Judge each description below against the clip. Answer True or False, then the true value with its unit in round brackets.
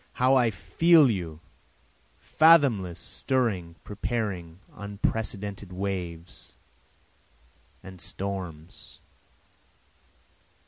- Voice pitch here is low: True (100 Hz)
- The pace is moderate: False (60 wpm)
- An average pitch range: True (4.8 semitones)